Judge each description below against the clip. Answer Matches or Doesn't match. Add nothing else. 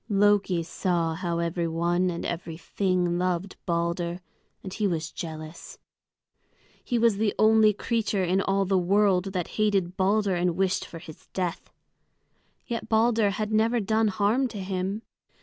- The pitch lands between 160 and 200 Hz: Matches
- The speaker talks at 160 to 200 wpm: Doesn't match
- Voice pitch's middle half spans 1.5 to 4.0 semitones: Matches